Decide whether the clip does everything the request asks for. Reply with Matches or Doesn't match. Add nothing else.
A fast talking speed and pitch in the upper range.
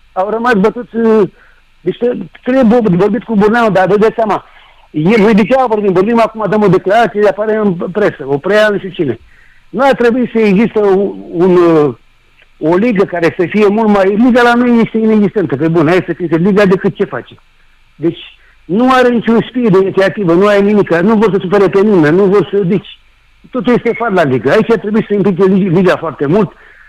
Matches